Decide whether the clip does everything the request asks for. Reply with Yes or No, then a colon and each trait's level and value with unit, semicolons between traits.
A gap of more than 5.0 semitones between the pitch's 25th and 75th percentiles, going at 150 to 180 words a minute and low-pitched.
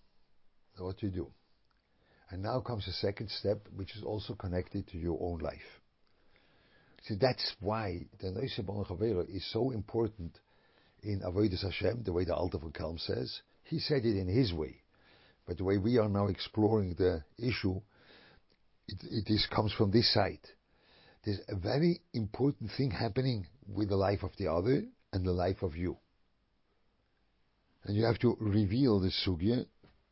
No: average, 3.6 semitones; average, 160 wpm; low, 100 Hz